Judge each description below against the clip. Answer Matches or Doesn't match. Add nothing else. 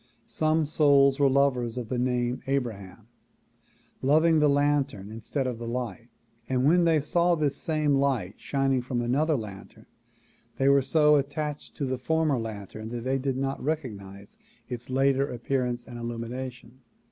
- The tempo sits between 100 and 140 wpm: Doesn't match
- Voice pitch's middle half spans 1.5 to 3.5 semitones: Matches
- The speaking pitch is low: Matches